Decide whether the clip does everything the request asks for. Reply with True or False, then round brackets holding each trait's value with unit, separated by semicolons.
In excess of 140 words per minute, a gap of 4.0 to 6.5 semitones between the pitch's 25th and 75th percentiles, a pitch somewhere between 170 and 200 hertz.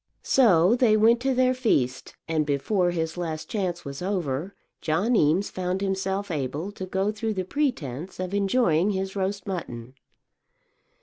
True (150 wpm; 4.4 semitones; 190 Hz)